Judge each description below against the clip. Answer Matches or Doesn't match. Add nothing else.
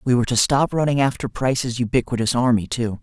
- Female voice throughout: Doesn't match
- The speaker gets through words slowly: Doesn't match